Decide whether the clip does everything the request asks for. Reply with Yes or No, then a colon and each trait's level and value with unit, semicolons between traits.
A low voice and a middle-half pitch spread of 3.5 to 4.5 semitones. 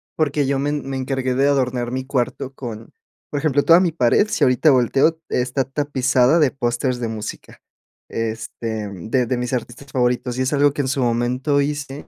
No: low, 130 Hz; narrow, 2.6 semitones